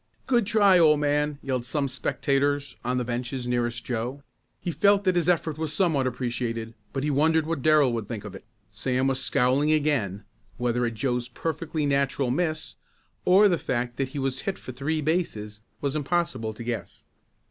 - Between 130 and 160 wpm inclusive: No, average, 180 wpm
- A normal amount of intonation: Yes, average, 4.2 semitones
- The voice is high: No, medium, 140 Hz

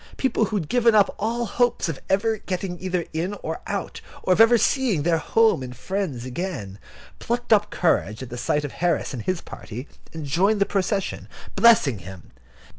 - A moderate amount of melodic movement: No, wide, 6.8 semitones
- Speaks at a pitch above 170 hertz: Yes, medium, 185 Hz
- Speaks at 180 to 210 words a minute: Yes, average, 190 wpm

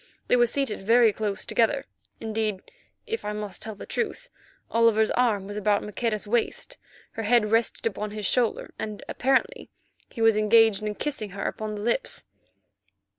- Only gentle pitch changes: Yes, narrow, 2.3 semitones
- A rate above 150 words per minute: Yes, average, 165 wpm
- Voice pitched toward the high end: Yes, high, 220 Hz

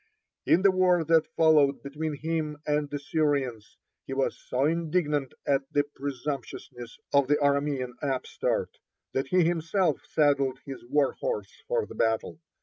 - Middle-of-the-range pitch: Yes, medium, 145 Hz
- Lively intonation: No, average, 2.9 semitones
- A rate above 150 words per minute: No, average, 145 wpm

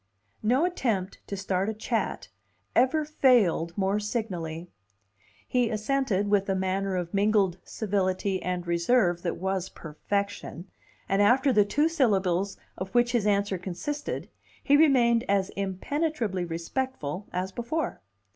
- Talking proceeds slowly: Yes, slow, 130 wpm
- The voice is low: No, high, 200 Hz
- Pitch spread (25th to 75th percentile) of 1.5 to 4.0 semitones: No, average, 4.6 semitones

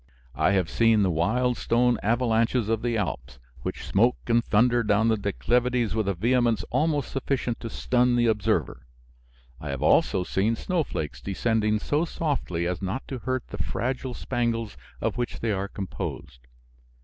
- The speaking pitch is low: Yes, low, 115 Hz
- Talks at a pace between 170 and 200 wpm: No, average, 160 wpm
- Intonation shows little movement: No, average, 3.8 semitones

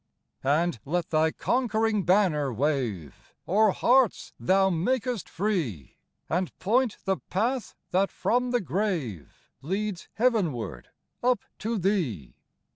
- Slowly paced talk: Yes, slow, 120 wpm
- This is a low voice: No, high, 190 Hz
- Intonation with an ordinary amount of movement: No, wide, 6.5 semitones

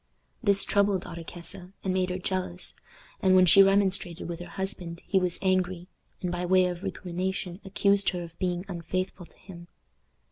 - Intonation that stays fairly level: Yes, narrow, 1.5 semitones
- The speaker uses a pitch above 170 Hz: Yes, medium, 185 Hz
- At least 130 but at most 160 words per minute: No, average, 170 wpm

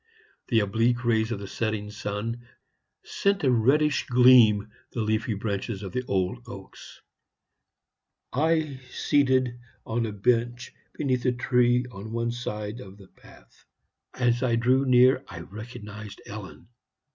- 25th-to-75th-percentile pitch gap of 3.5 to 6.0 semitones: No, average, 3.1 semitones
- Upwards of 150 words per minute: No, slow, 135 wpm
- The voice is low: Yes, low, 115 Hz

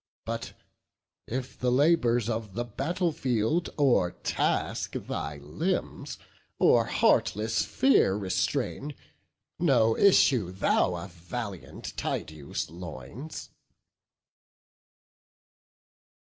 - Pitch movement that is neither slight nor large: No, wide, 7.3 semitones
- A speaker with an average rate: No, slow, 80 wpm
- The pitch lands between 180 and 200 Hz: No, low, 115 Hz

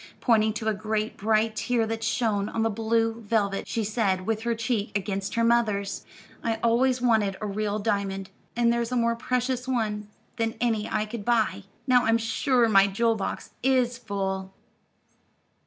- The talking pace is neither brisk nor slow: Yes, average, 170 wpm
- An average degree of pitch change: No, narrow, 2.3 semitones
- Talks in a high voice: Yes, high, 225 Hz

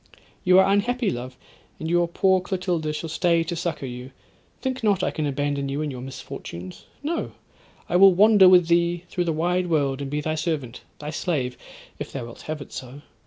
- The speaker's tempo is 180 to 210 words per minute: Yes, average, 200 wpm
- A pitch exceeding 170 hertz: No, medium, 165 Hz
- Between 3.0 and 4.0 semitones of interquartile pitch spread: No, average, 4.5 semitones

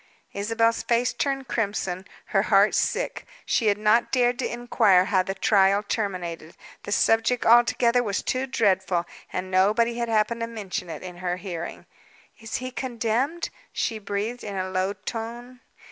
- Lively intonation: No, average, 3.9 semitones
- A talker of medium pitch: No, high, 220 Hz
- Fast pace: No, average, 160 wpm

